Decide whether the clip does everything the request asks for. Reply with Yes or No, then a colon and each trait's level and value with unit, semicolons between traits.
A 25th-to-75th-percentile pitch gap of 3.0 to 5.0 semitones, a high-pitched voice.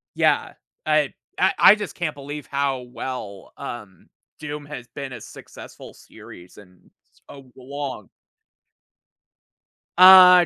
No: average, 3.6 semitones; medium, 140 Hz